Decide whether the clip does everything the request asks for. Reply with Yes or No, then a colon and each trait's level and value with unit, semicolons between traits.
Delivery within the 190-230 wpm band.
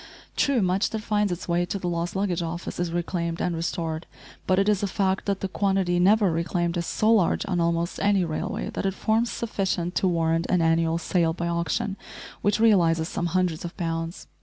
Yes: fast, 205 wpm